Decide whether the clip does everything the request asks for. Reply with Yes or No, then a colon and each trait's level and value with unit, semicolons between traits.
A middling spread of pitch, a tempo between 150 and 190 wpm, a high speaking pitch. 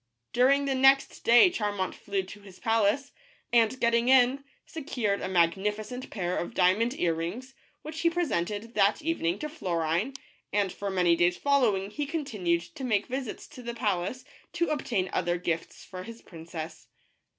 No: wide, 6.2 semitones; average, 165 wpm; high, 210 Hz